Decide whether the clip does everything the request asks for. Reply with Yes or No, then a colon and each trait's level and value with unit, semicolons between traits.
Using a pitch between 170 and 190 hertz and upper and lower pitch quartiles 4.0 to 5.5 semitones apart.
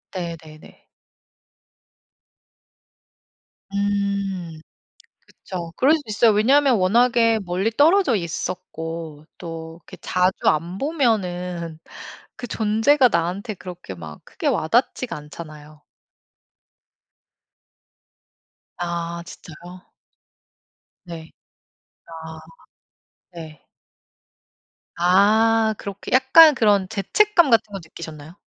Yes: medium, 185 Hz; average, 5.2 semitones